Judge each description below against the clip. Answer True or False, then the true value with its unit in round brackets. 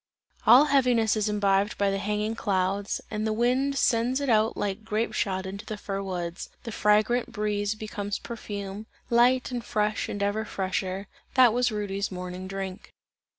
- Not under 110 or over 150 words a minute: False (165 wpm)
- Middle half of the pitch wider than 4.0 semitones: False (2.8 semitones)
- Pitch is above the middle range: True (210 Hz)